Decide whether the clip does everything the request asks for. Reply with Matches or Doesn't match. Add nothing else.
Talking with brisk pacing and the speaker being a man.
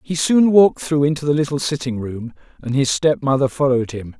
Matches